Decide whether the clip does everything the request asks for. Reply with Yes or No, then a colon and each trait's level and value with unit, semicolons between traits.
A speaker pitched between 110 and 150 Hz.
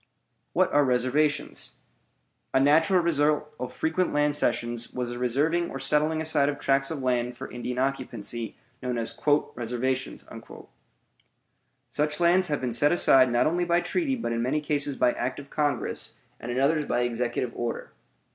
Yes: low, 135 Hz